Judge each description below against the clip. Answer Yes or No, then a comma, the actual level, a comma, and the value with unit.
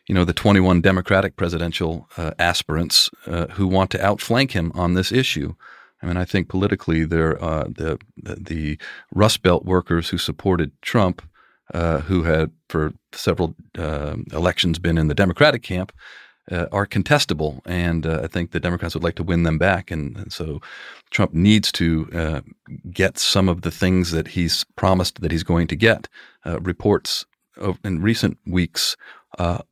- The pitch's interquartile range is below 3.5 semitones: Yes, narrow, 2.6 semitones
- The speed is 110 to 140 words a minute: No, average, 175 wpm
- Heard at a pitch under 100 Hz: Yes, very low, 90 Hz